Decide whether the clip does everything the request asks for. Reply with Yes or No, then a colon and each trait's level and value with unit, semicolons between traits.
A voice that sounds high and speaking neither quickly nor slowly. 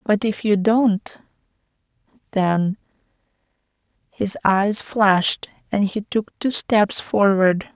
No: high, 205 Hz; slow, 110 wpm